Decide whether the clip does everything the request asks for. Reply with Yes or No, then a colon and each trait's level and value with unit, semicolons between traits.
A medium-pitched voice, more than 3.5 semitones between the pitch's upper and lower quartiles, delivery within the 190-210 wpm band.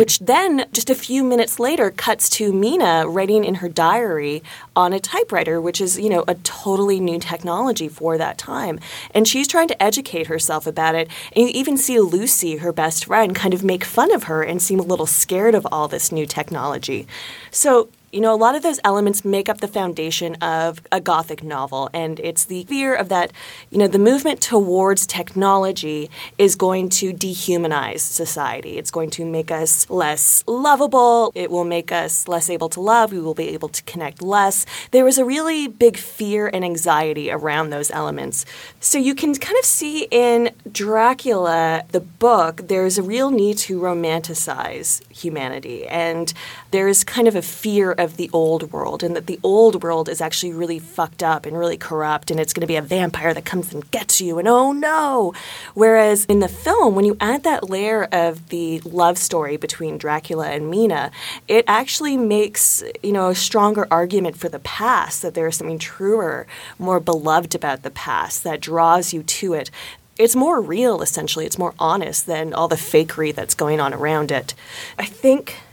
Yes: medium, 180 Hz; average, 5.1 semitones; average, 195 wpm